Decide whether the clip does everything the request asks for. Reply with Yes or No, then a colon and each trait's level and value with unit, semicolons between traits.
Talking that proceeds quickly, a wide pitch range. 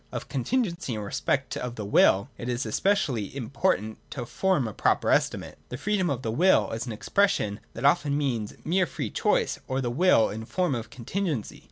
Yes: fast, 210 wpm; wide, 7.6 semitones